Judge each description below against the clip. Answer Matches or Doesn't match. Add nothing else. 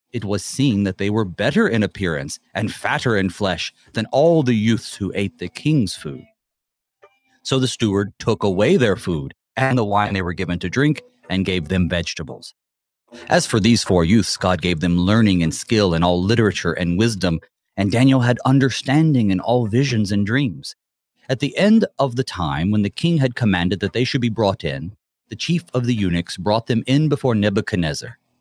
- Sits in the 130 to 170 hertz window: Doesn't match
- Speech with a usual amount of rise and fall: Doesn't match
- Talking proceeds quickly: Doesn't match